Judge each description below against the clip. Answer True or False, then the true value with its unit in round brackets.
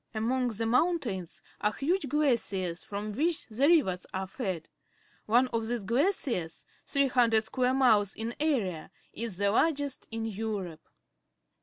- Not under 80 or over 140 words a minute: True (135 wpm)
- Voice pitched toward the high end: True (225 Hz)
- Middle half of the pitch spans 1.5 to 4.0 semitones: False (5.0 semitones)